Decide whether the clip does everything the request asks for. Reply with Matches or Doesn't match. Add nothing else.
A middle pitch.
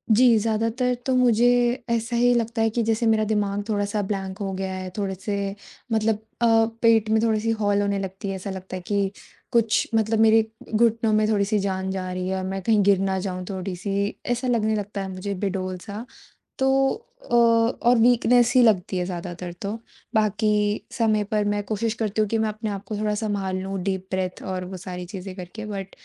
Doesn't match